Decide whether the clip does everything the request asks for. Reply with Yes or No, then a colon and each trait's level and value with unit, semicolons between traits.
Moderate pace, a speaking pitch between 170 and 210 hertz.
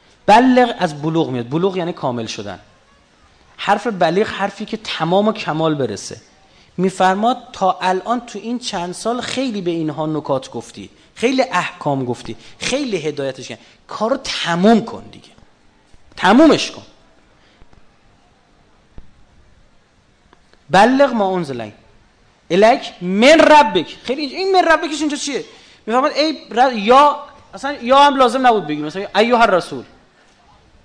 Yes: average, 130 wpm; medium, 185 Hz